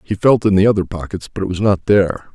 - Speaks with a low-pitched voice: Yes, very low, 95 Hz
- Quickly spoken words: Yes, fast, 280 wpm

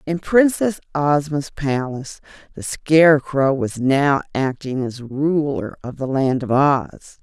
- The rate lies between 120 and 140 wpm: Yes, slow, 135 wpm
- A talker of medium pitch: Yes, medium, 145 Hz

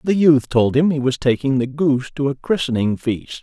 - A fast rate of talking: Yes, fast, 230 wpm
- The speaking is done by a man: Yes, male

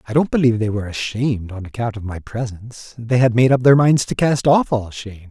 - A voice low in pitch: Yes, low, 120 Hz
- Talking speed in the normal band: No, fast, 250 wpm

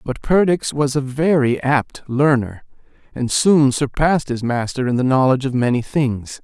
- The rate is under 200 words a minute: Yes, average, 170 wpm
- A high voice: No, low, 135 Hz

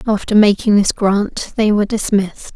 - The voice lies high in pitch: Yes, high, 205 Hz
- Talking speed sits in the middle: Yes, average, 165 wpm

